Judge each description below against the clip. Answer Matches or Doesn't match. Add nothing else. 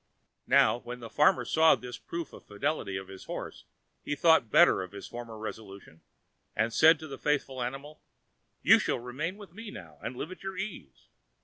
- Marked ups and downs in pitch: Matches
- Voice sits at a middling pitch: Doesn't match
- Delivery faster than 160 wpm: Matches